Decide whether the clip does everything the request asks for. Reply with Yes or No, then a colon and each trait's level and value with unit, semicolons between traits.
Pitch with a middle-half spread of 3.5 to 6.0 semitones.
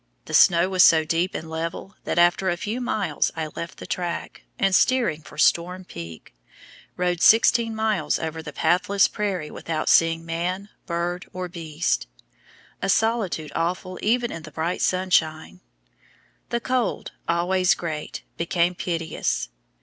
No: narrow, 2.6 semitones